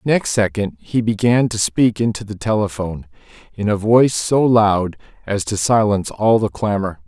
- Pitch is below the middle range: Yes, low, 105 Hz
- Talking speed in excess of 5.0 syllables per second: No, 4.9 syllables/s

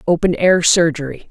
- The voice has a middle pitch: Yes, medium, 170 Hz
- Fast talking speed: No, average, 140 wpm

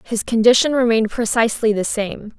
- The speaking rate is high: No, average, 150 wpm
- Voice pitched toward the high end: Yes, high, 225 Hz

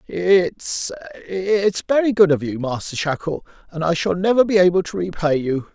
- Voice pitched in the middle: Yes, medium, 180 Hz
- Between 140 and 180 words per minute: Yes, average, 165 wpm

